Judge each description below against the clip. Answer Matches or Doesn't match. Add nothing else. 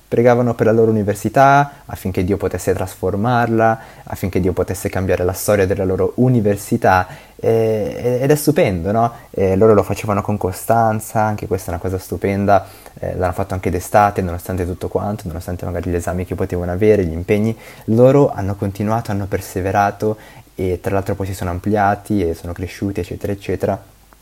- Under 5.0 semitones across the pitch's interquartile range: Matches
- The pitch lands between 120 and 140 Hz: Doesn't match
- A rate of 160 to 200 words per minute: Matches